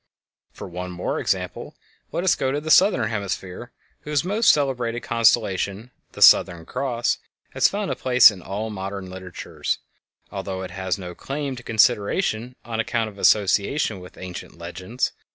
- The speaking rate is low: No, average, 155 wpm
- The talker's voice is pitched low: Yes, low, 110 Hz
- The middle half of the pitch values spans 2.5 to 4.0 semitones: No, average, 5.2 semitones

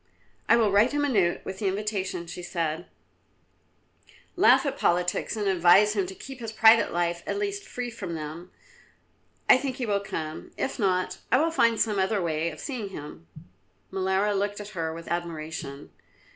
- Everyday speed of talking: Yes, average, 180 wpm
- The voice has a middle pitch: No, high, 195 Hz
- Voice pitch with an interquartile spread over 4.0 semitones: Yes, average, 4.5 semitones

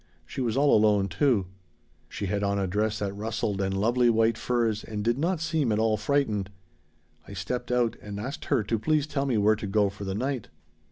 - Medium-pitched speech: No, low, 110 Hz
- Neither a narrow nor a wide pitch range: Yes, average, 3.6 semitones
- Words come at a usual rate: No, fast, 215 wpm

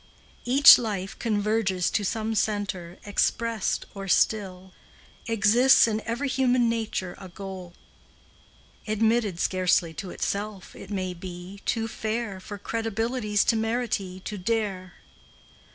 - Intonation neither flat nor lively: Yes, average, 3.2 semitones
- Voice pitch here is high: Yes, high, 210 Hz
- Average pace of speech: No, slow, 115 wpm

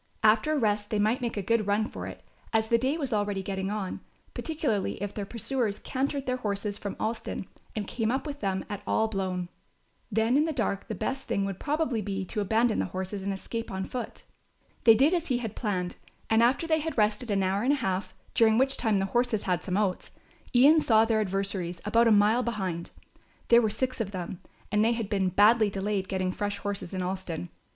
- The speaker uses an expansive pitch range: No, average, 3.5 semitones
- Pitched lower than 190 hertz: No, high, 215 Hz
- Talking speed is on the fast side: Yes, fast, 220 wpm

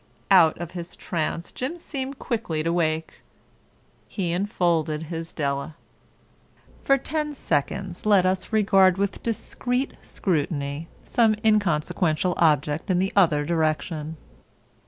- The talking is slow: Yes, slow, 115 wpm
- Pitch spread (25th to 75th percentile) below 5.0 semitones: Yes, average, 4.4 semitones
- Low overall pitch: No, medium, 175 Hz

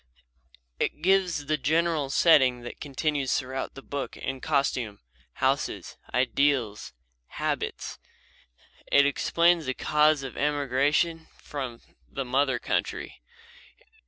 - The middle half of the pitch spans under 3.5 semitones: Yes, average, 2.8 semitones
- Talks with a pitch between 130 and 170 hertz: Yes, medium, 140 Hz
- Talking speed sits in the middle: No, slow, 110 wpm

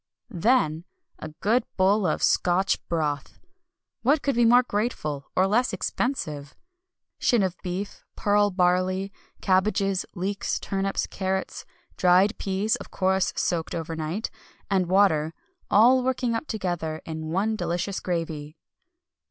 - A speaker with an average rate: No, slow, 125 wpm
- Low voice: No, high, 190 Hz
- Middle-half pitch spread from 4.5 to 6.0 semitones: No, average, 3.7 semitones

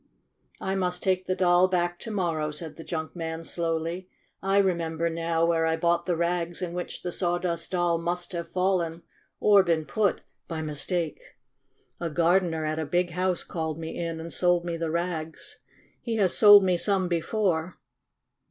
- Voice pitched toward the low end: No, medium, 170 Hz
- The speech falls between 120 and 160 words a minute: No, average, 175 wpm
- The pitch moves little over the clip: Yes, narrow, 1.8 semitones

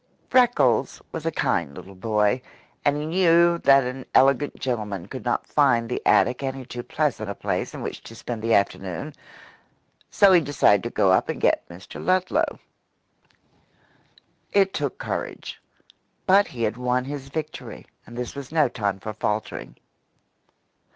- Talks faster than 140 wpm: Yes, average, 155 wpm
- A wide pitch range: Yes, wide, 5.9 semitones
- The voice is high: No, low, 125 Hz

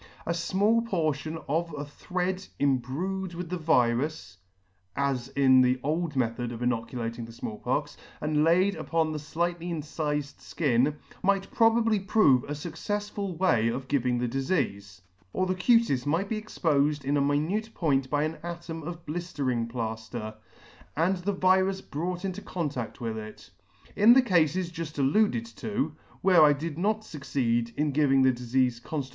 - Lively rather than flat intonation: Yes, wide, 5.8 semitones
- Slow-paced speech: No, average, 165 wpm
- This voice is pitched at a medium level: Yes, medium, 155 Hz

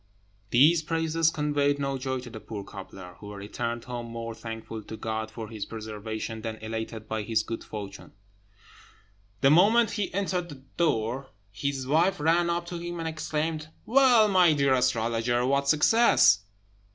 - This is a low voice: Yes, low, 130 Hz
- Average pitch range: No, wide, 6.6 semitones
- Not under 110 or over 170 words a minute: Yes, average, 160 wpm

